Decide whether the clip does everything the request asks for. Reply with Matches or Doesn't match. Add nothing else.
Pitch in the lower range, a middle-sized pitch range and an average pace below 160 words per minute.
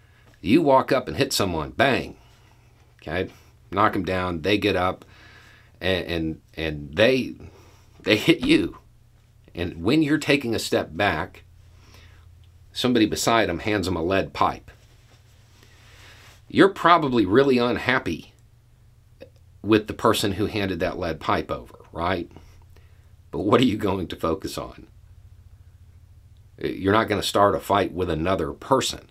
Matches